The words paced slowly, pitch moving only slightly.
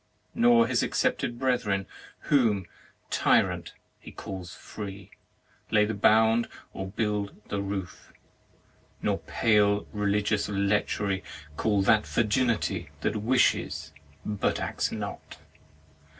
Yes: slow, 105 wpm; narrow, 2.2 semitones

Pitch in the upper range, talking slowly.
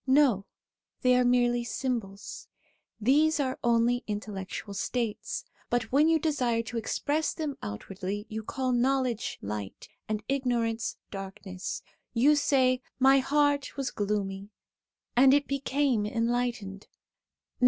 Yes: high, 240 Hz; slow, 120 wpm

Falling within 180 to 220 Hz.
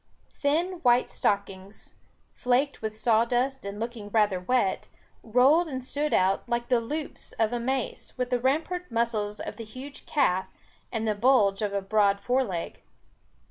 No: high, 235 Hz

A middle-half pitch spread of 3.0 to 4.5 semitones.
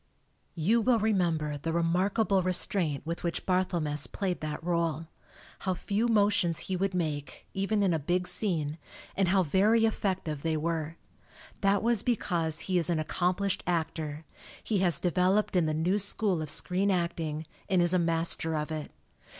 Yes: average, 3.4 semitones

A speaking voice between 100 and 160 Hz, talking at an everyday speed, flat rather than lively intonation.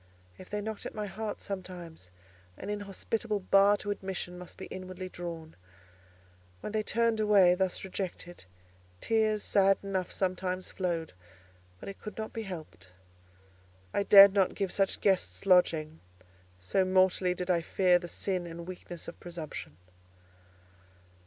No: medium, 185 Hz; average, 145 wpm; narrow, 2.3 semitones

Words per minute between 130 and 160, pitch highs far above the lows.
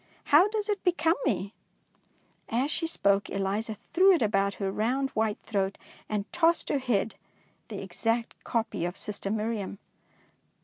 Yes: average, 150 wpm; wide, 6.5 semitones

